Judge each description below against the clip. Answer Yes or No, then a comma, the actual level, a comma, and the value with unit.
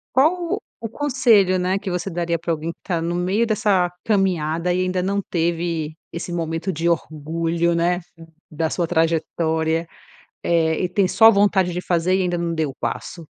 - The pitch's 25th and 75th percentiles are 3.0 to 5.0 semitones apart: No, narrow, 2.6 semitones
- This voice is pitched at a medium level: Yes, medium, 175 Hz